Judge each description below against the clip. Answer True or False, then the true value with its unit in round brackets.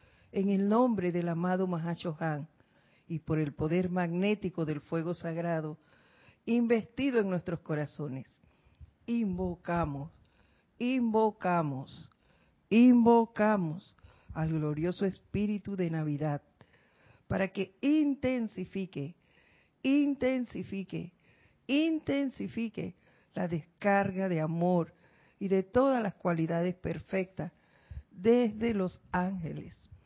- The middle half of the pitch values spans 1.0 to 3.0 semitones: False (5.0 semitones)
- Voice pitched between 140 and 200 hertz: True (185 Hz)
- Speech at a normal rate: False (90 wpm)